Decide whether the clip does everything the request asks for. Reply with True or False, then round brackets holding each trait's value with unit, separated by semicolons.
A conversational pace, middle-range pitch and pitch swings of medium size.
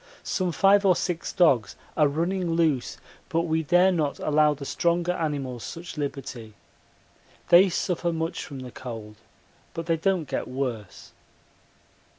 True (145 wpm; 160 Hz; 4.2 semitones)